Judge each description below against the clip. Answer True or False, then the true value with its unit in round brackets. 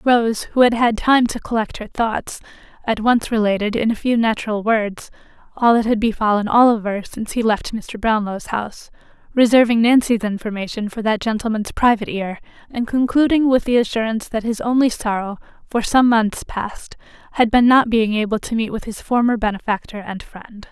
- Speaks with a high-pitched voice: True (225 Hz)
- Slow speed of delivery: False (180 wpm)